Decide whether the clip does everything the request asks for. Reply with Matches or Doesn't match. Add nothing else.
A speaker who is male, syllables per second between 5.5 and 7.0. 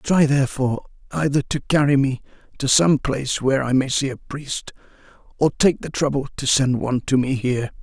Matches